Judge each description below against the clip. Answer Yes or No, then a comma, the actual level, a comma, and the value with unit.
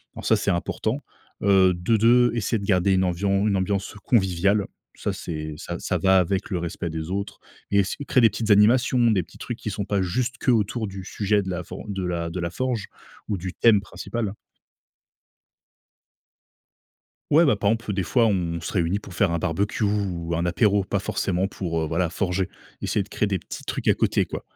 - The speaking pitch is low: Yes, low, 100 Hz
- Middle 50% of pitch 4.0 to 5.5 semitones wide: No, average, 3.0 semitones